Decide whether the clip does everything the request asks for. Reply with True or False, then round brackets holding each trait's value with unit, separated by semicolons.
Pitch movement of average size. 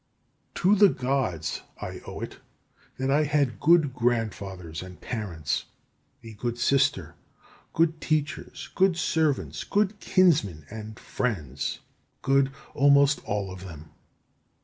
False (8.0 semitones)